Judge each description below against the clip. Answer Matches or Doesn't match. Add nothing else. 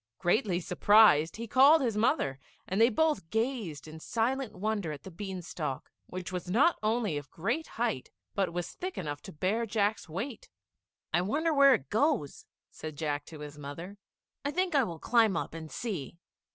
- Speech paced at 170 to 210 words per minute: Matches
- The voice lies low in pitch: Doesn't match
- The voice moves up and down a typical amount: Doesn't match